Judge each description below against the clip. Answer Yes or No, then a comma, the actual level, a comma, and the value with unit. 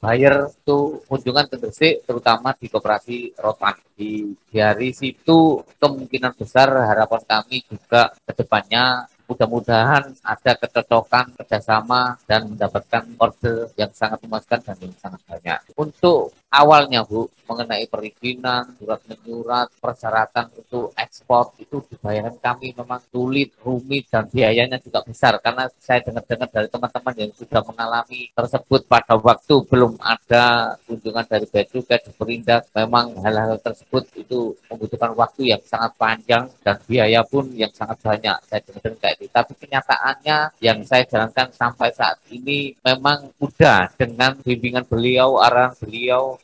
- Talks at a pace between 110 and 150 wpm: Yes, average, 135 wpm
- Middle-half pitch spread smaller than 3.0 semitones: Yes, narrow, 2.4 semitones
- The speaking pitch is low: Yes, low, 120 Hz